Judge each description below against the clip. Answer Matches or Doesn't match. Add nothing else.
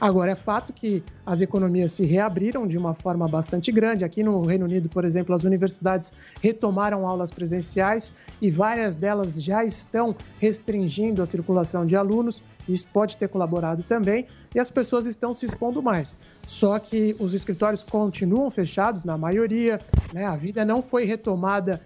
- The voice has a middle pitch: Doesn't match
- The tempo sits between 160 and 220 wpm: Matches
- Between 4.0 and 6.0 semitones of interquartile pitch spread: Doesn't match